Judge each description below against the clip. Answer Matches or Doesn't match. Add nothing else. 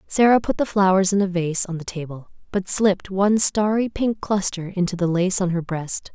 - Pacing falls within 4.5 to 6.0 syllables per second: Matches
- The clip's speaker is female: Matches